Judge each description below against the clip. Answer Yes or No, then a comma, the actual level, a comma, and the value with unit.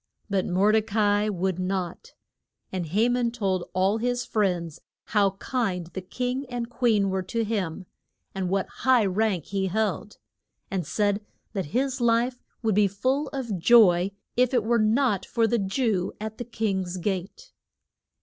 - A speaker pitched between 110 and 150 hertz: No, high, 210 Hz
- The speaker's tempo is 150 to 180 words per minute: Yes, average, 165 wpm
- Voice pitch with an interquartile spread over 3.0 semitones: Yes, average, 3.9 semitones